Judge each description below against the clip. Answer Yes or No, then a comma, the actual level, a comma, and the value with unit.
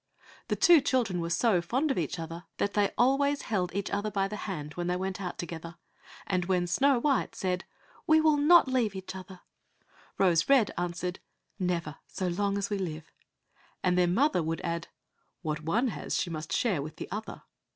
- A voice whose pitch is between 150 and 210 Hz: Yes, high, 190 Hz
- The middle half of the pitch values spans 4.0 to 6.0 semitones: Yes, average, 4.9 semitones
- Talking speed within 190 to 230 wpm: Yes, average, 195 wpm